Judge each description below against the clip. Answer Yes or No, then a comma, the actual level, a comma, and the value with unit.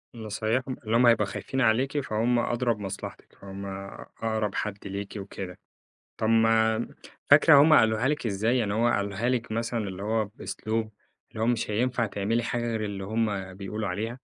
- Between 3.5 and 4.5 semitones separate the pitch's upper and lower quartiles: No, narrow, 2.6 semitones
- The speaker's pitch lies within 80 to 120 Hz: Yes, low, 110 Hz